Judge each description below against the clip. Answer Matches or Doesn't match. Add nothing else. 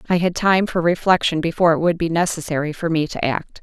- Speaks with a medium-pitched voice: Matches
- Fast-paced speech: Matches